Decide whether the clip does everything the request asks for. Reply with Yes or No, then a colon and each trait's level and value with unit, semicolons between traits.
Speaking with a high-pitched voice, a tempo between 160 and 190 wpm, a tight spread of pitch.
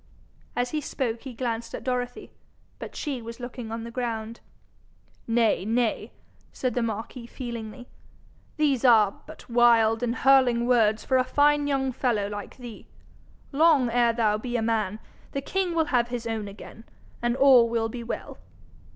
Yes: high, 240 Hz; average, 165 wpm; narrow, 2.3 semitones